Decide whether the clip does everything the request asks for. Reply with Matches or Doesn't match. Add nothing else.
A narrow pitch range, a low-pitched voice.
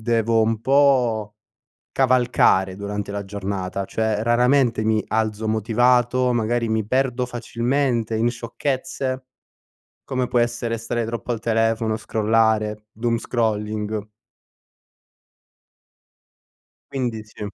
Matches